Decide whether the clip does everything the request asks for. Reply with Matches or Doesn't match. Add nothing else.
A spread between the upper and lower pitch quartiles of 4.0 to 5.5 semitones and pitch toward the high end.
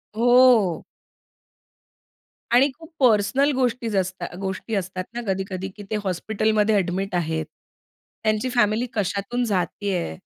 Matches